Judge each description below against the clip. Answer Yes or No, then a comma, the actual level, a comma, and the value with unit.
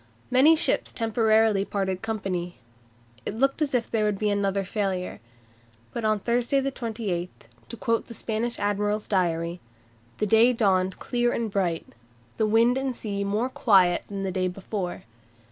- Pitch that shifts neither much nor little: Yes, average, 3.3 semitones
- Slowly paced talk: No, average, 160 wpm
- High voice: Yes, high, 210 Hz